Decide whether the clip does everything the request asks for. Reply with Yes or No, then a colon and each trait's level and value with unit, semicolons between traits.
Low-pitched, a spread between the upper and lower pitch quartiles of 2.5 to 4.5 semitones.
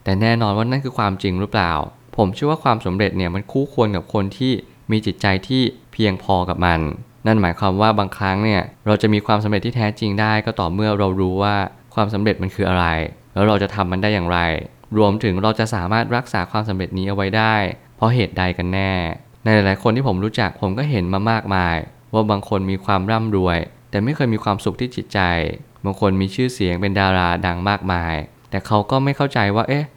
Yes: low, 105 Hz; average, 3.0 semitones